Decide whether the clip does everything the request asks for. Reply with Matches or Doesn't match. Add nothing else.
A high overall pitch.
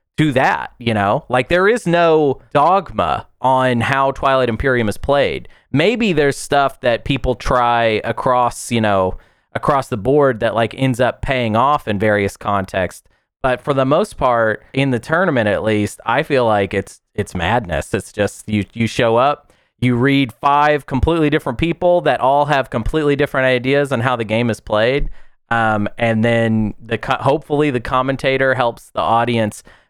Doesn't match